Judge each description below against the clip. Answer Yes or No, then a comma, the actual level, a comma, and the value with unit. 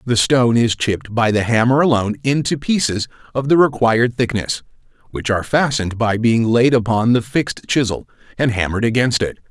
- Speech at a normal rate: Yes, average, 175 wpm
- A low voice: Yes, low, 120 Hz